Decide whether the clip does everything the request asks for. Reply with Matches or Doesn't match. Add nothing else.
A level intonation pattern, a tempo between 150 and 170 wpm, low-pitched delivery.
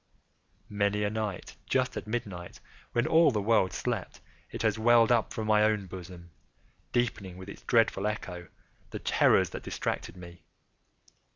Doesn't match